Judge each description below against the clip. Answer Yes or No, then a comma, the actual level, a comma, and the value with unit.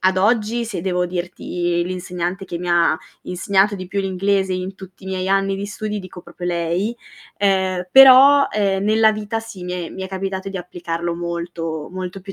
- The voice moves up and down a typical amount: No, narrow, 2.2 semitones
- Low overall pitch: No, high, 190 Hz